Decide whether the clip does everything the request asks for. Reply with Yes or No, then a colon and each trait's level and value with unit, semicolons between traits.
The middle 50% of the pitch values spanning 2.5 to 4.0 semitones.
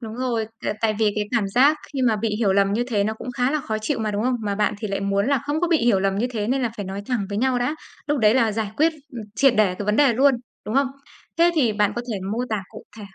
Yes: average, 3.7 semitones